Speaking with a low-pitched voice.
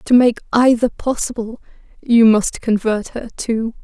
No: high, 230 Hz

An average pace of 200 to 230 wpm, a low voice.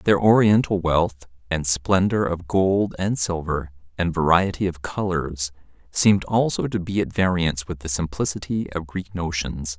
No: average, 155 wpm; very low, 85 Hz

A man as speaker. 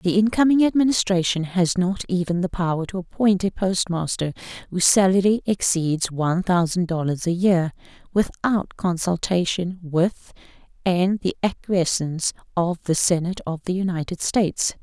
No: female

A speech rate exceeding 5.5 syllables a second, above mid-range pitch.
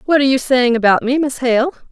Yes: 6.2 syllables/s; very high, 260 Hz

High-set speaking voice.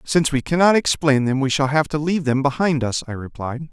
No: medium, 145 Hz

